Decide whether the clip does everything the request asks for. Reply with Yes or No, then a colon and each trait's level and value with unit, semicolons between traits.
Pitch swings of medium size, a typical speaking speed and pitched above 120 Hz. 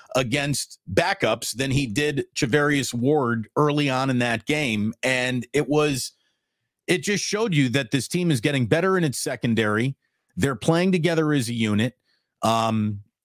Yes: average, 4.2 semitones; average, 160 wpm; medium, 140 Hz